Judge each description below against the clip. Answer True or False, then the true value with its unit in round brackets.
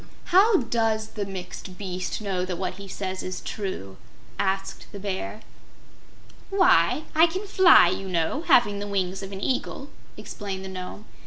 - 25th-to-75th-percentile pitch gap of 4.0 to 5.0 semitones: False (3.5 semitones)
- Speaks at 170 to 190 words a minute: False (160 wpm)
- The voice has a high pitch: True (200 Hz)